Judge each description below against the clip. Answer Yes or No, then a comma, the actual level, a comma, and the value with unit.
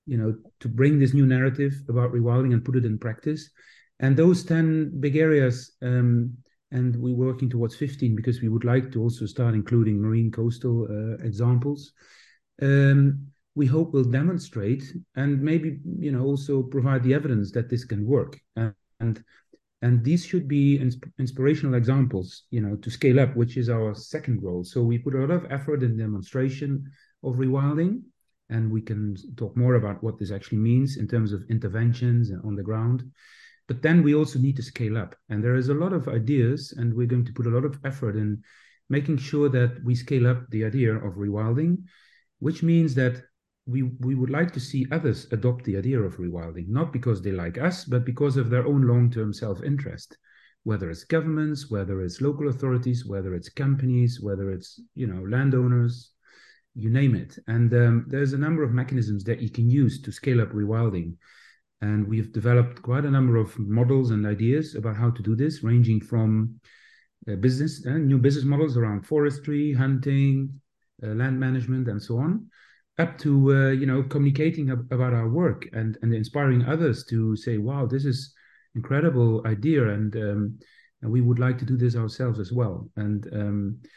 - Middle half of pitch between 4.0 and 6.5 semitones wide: No, average, 3.5 semitones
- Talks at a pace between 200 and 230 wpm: No, average, 190 wpm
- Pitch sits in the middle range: No, low, 125 Hz